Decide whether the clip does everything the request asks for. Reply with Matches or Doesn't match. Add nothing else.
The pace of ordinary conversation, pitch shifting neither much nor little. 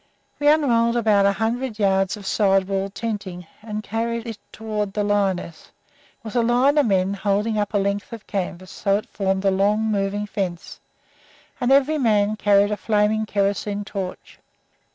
Doesn't match